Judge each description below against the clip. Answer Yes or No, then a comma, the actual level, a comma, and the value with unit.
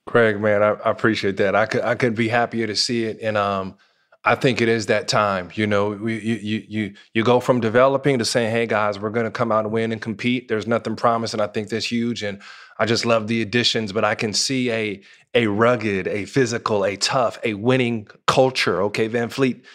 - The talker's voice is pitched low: Yes, low, 115 Hz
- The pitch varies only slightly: Yes, narrow, 1.9 semitones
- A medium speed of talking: No, fast, 230 wpm